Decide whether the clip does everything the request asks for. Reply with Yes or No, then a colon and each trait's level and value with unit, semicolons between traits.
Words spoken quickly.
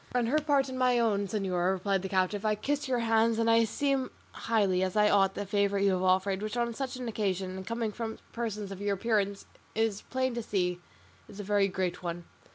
Yes: fast, 230 wpm